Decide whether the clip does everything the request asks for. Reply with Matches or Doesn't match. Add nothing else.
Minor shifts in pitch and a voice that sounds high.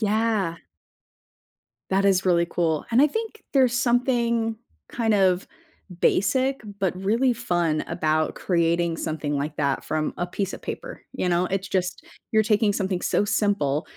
Doesn't match